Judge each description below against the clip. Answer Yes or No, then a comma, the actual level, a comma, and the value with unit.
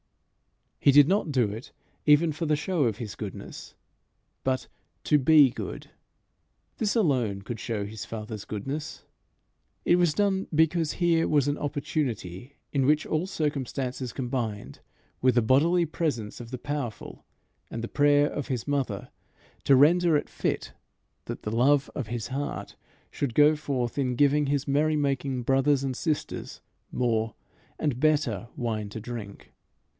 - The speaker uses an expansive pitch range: No, average, 4.1 semitones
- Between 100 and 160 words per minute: Yes, average, 150 wpm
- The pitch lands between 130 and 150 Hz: Yes, medium, 140 Hz